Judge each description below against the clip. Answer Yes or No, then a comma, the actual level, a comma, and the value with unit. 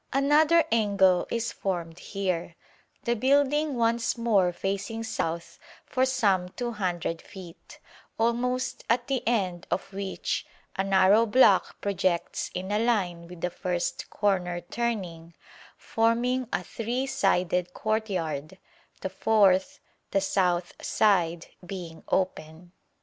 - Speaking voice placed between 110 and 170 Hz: No, high, 195 Hz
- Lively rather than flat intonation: No, average, 4.6 semitones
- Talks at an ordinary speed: No, slow, 115 wpm